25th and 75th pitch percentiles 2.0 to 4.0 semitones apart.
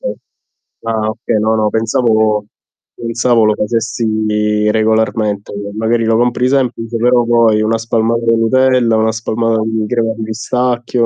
No: narrow, 1.4 semitones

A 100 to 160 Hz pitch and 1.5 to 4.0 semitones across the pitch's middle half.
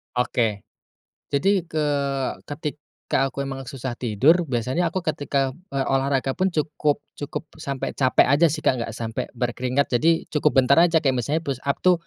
Yes: medium, 140 Hz; average, 3.4 semitones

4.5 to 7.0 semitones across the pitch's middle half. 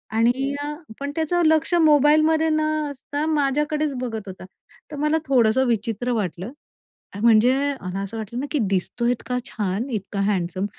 Yes: wide, 5.5 semitones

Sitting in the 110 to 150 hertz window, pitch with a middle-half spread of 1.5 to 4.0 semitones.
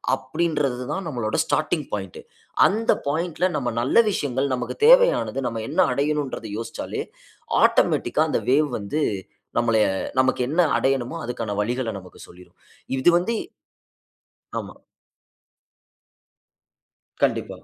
No: low, 135 Hz; average, 4.9 semitones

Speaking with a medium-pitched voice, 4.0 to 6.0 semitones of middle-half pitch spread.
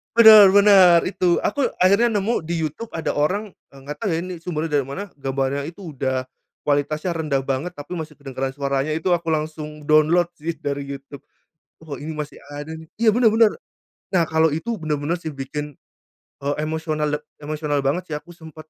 No: medium, 155 Hz; average, 3.6 semitones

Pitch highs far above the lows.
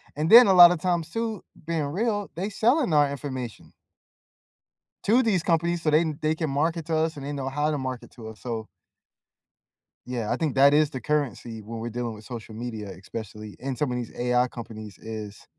Yes: wide, 6.0 semitones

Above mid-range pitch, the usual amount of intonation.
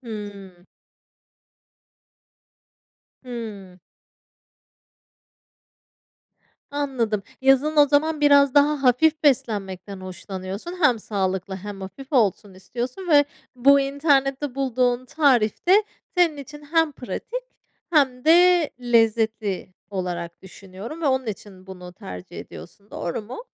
No: high, 245 Hz; wide, 6.7 semitones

